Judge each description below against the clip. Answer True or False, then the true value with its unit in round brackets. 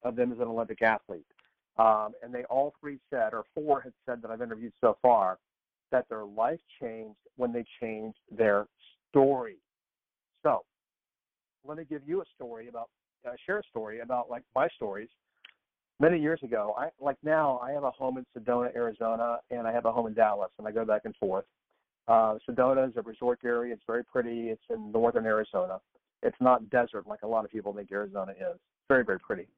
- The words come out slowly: False (200 wpm)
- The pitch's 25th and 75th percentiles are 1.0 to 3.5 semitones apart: True (2.5 semitones)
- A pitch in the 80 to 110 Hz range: False (120 Hz)